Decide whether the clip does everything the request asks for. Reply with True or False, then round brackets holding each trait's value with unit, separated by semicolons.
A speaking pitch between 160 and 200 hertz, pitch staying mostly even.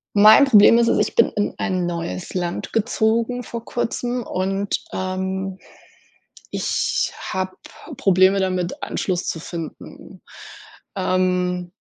False (190 Hz; 3.2 semitones)